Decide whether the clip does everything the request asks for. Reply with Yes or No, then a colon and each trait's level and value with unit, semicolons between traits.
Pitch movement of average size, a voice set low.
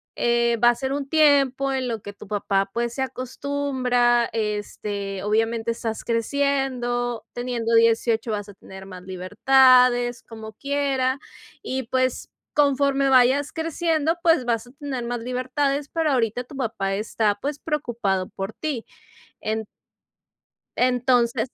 No: average, 3.4 semitones; high, 245 Hz